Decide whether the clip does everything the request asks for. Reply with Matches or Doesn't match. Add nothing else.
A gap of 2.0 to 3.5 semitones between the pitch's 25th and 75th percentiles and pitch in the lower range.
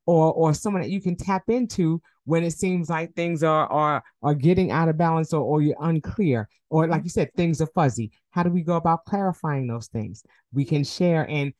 Doesn't match